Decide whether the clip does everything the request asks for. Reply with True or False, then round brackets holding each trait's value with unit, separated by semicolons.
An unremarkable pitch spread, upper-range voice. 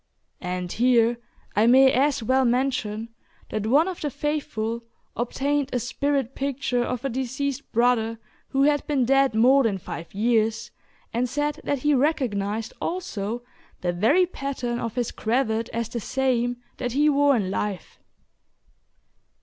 True (3.6 semitones; 245 Hz)